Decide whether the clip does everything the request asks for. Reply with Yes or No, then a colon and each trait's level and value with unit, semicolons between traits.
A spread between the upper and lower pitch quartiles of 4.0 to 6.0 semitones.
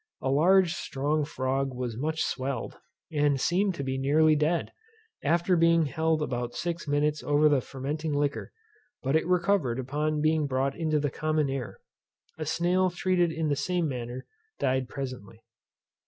No: average, 3.3 semitones